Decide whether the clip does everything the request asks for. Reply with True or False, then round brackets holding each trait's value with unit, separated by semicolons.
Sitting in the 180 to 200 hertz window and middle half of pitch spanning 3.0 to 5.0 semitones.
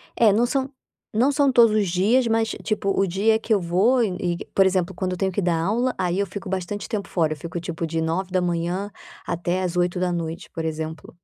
True (185 Hz; 3.7 semitones)